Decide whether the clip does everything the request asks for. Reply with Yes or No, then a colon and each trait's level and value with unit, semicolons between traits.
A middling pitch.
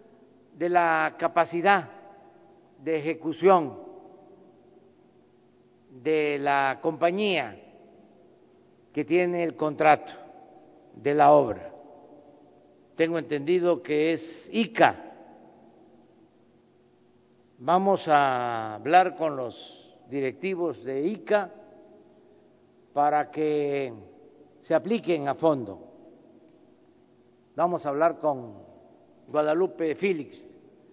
Yes: medium, 155 Hz